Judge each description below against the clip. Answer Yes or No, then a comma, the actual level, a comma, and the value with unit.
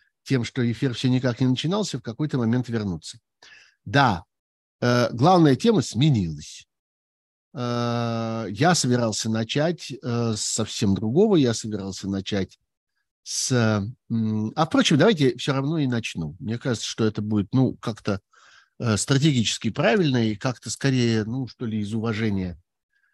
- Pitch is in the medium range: No, low, 115 Hz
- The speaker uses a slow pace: No, average, 125 wpm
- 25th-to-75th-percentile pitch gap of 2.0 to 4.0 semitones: Yes, average, 3.5 semitones